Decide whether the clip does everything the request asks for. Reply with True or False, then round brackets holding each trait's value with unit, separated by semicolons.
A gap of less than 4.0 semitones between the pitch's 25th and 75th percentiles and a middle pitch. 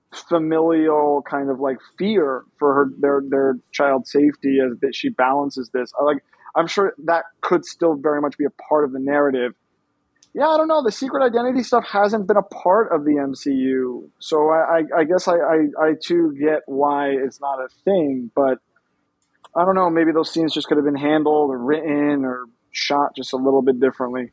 True (3.3 semitones; 145 Hz)